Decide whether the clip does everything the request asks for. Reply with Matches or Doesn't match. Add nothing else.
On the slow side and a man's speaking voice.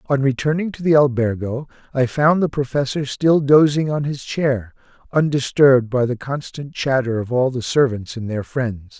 Doesn't match